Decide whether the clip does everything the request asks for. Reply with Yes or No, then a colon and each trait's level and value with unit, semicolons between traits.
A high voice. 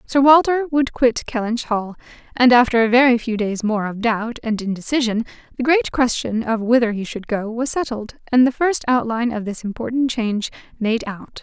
Yes: high, 235 Hz